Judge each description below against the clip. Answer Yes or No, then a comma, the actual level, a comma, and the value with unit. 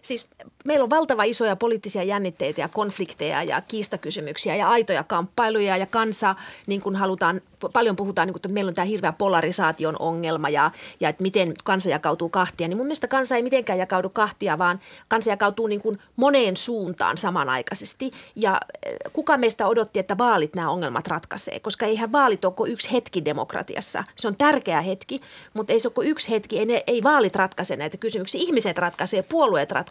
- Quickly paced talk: Yes, fast, 175 wpm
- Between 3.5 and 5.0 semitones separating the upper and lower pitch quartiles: Yes, average, 4.3 semitones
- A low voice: No, high, 205 Hz